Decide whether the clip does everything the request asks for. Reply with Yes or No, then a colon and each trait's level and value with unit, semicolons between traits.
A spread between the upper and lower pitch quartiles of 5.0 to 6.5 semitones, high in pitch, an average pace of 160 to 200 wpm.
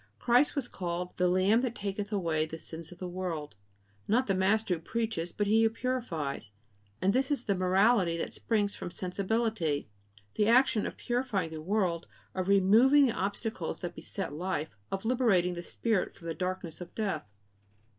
No: average, 4.4 semitones; high, 195 Hz; average, 175 wpm